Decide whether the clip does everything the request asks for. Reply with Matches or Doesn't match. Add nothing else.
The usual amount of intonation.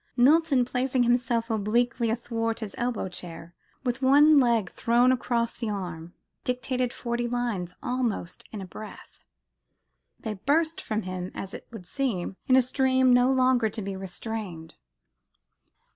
Matches